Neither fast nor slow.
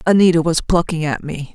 Yes: average, 195 wpm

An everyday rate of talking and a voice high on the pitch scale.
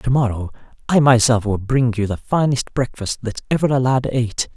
No: average, 195 wpm; low, 120 Hz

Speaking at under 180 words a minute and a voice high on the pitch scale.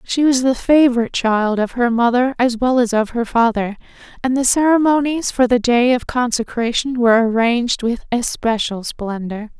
Yes: average, 170 wpm; high, 240 Hz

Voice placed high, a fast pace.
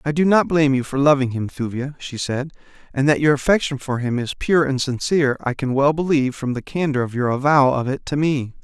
No: medium, 140 Hz; fast, 245 wpm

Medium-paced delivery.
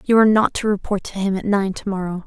No: fast, 265 wpm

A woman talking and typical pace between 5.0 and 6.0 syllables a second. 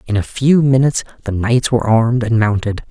No: male; 5.9 syllables/s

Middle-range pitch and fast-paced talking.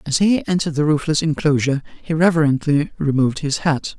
No: medium, 150 Hz; average, 165 wpm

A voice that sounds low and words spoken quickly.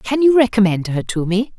No: high, 220 Hz; fast, 230 wpm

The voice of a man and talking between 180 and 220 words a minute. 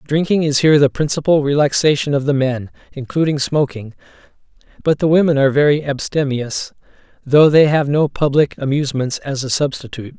No: male; average, 155 wpm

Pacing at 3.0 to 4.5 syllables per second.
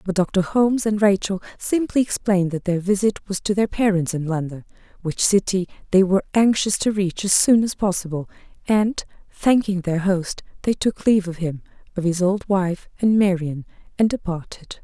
No: 5.1 syllables/s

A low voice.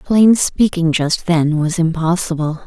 No: medium, 170 Hz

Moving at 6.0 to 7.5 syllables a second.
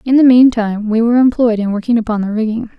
Yes: 6.5 syllables/s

